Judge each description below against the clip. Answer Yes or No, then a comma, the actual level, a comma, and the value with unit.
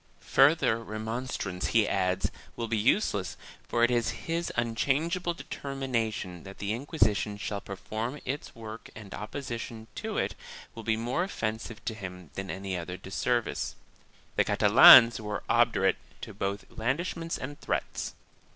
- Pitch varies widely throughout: No, average, 4.3 semitones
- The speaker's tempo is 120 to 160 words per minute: Yes, average, 145 wpm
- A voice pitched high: No, low, 115 Hz